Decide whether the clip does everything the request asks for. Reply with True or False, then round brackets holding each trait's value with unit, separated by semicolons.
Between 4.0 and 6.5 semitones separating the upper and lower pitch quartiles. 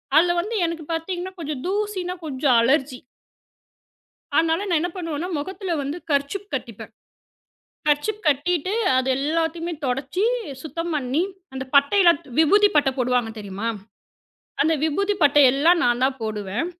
True (4.9 semitones)